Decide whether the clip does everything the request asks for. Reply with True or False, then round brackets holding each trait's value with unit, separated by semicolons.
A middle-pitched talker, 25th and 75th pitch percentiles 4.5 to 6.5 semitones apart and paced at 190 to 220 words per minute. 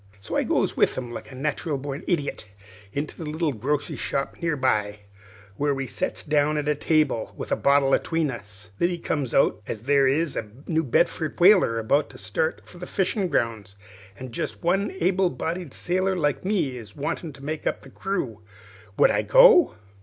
True (145 Hz; 4.8 semitones; 195 wpm)